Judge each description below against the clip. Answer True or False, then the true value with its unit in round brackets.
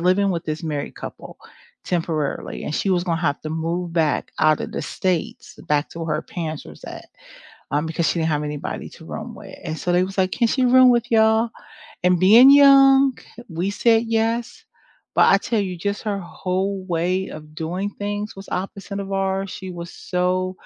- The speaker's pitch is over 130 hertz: True (185 Hz)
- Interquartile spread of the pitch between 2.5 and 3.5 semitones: False (3.9 semitones)